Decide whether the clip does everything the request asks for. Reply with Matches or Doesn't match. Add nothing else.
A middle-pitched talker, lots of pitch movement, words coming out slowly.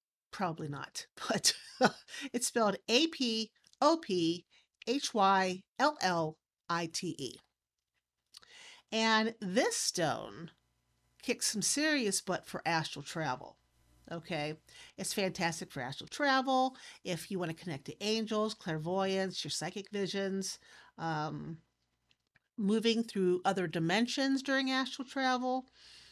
Doesn't match